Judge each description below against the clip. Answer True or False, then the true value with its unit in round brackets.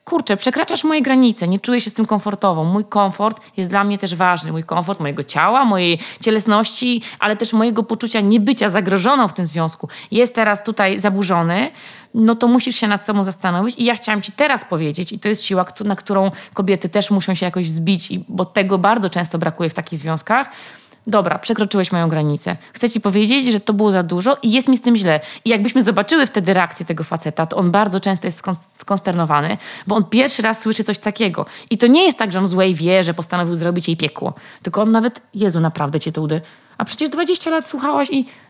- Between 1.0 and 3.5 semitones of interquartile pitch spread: False (4.2 semitones)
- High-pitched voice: True (205 Hz)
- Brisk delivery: True (210 wpm)